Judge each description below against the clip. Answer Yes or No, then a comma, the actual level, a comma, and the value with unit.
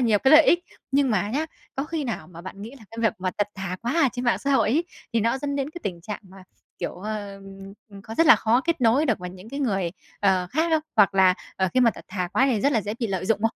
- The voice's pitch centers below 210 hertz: No, high, 225 Hz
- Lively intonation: Yes, wide, 5.8 semitones